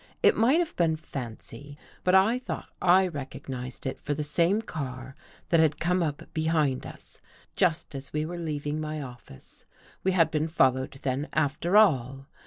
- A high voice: No, medium, 155 Hz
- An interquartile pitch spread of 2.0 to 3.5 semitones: No, average, 4.2 semitones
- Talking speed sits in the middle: Yes, average, 175 wpm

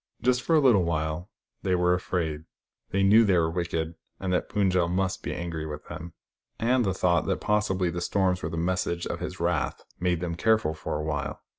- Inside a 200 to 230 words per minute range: Yes, fast, 205 wpm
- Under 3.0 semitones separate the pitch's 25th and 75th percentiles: Yes, narrow, 2.5 semitones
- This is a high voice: No, very low, 90 Hz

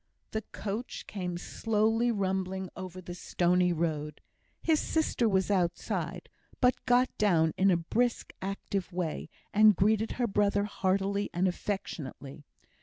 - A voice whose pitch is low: No, high, 195 Hz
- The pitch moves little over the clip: No, average, 3.2 semitones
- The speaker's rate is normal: No, slow, 130 wpm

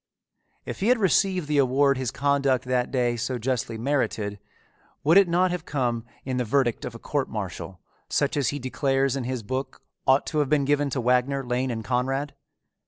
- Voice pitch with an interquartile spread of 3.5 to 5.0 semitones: No, average, 2.7 semitones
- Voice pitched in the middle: No, low, 130 Hz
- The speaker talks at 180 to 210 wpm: Yes, average, 195 wpm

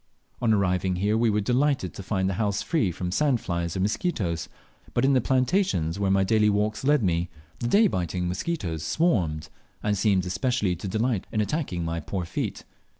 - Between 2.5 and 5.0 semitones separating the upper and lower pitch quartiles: No, wide, 5.4 semitones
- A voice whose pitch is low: Yes, low, 100 Hz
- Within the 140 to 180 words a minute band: No, average, 190 wpm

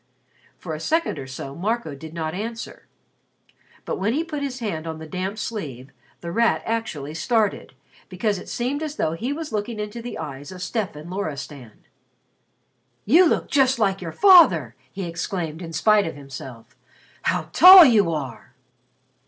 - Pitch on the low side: No, high, 190 Hz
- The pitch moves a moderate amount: No, wide, 6.8 semitones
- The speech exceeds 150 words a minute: Yes, average, 165 wpm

